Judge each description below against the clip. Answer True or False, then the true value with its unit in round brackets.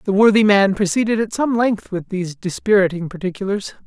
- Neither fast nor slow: True (170 wpm)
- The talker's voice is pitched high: True (200 Hz)